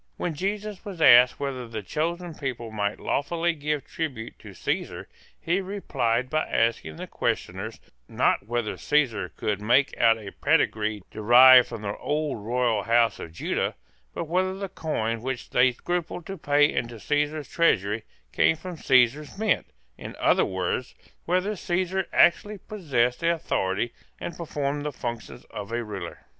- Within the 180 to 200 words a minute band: No, average, 155 wpm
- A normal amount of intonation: No, wide, 6.6 semitones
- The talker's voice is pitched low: Yes, low, 130 Hz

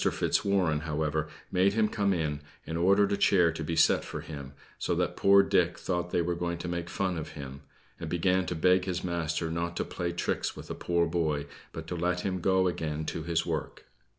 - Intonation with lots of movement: No, narrow, 2.4 semitones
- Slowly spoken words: No, fast, 205 wpm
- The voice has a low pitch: Yes, very low, 85 Hz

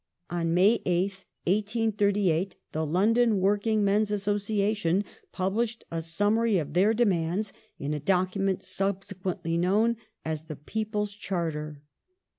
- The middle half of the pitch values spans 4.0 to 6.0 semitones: No, average, 3.4 semitones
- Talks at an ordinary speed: No, slow, 115 wpm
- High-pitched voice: Yes, high, 195 Hz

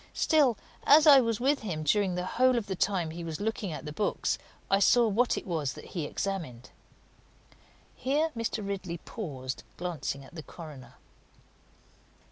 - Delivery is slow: No, average, 165 wpm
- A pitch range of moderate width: No, wide, 6.5 semitones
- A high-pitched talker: Yes, high, 195 Hz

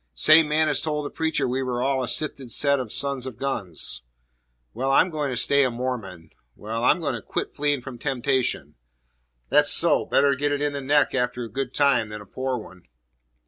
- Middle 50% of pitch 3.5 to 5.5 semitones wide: No, average, 2.8 semitones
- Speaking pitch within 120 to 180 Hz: Yes, low, 135 Hz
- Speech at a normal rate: No, fast, 210 wpm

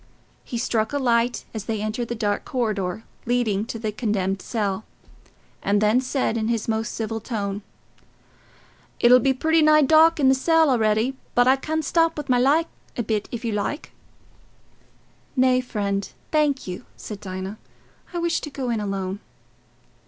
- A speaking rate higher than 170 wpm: No, average, 165 wpm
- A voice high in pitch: Yes, high, 235 Hz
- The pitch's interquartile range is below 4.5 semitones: Yes, average, 4.1 semitones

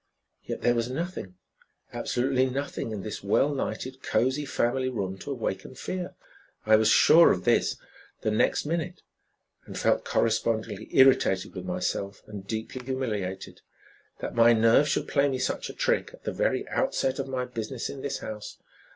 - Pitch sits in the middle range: No, low, 125 Hz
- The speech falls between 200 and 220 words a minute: No, average, 165 wpm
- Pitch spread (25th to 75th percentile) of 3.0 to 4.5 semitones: Yes, average, 4.0 semitones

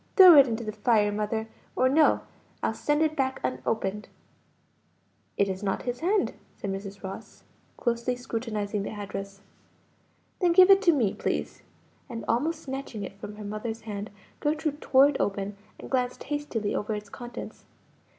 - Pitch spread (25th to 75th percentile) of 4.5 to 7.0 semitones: Yes, average, 5.0 semitones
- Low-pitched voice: No, high, 225 Hz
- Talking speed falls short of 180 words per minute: Yes, average, 160 wpm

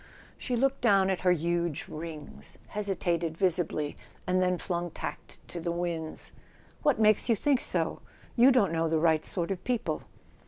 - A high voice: No, medium, 175 Hz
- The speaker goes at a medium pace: Yes, average, 165 wpm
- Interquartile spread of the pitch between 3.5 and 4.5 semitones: Yes, average, 3.9 semitones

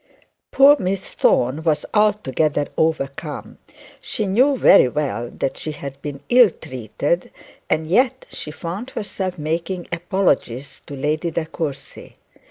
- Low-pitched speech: No, medium, 160 Hz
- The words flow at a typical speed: No, slow, 130 wpm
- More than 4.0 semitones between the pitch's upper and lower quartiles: Yes, average, 5.2 semitones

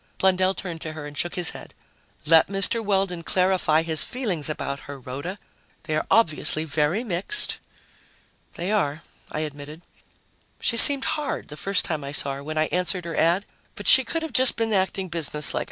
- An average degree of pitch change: Yes, average, 4.4 semitones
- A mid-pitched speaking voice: Yes, medium, 175 Hz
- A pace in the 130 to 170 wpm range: No, average, 185 wpm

